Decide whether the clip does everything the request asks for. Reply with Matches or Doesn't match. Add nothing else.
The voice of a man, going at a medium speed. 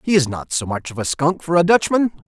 Doesn't match